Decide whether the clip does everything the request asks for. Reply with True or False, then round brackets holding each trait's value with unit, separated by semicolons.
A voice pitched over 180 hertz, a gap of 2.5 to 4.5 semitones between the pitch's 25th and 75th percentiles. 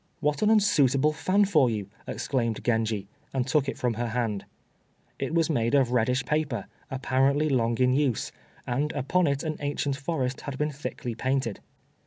False (135 Hz; 3.7 semitones)